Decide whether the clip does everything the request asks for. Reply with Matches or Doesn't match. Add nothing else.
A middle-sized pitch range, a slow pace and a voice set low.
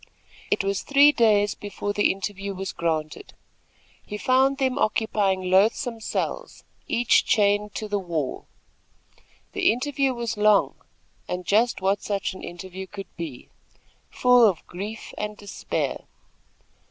Doesn't match